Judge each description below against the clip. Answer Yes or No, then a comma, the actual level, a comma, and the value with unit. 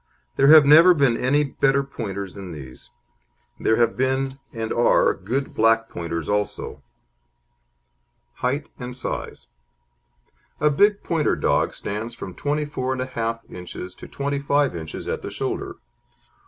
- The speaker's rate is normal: No, slow, 130 wpm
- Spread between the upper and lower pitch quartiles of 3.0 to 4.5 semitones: No, average, 5.2 semitones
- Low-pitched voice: Yes, low, 130 Hz